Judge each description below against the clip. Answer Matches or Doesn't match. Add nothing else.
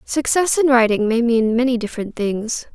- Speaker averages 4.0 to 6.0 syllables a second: Matches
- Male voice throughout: Doesn't match